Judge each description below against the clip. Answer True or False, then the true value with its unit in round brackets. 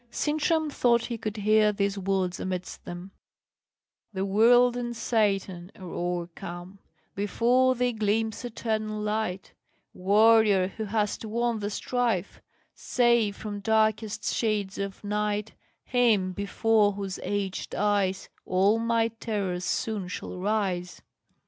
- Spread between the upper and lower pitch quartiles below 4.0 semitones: True (2.6 semitones)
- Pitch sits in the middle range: False (210 Hz)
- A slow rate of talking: True (120 wpm)